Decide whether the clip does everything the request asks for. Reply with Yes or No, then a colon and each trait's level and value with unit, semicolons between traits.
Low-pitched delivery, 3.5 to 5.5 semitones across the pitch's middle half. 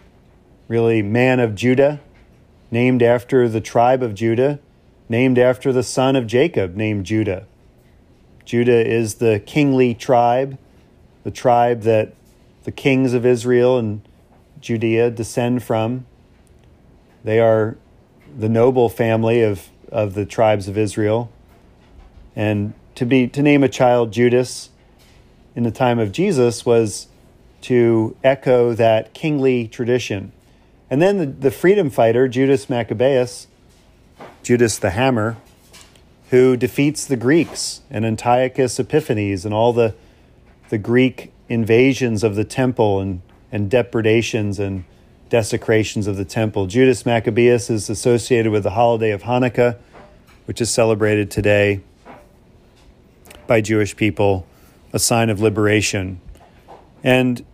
No: low, 115 Hz; average, 2.8 semitones